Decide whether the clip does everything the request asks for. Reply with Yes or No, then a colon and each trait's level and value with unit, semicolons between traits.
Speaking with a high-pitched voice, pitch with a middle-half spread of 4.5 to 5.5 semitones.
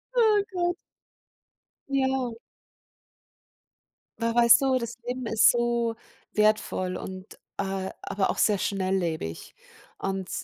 Yes: high, 230 Hz; average, 4.9 semitones